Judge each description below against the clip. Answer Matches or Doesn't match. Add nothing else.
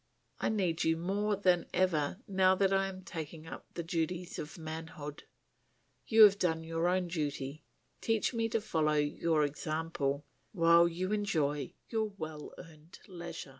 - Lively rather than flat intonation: Doesn't match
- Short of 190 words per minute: Matches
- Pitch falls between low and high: Matches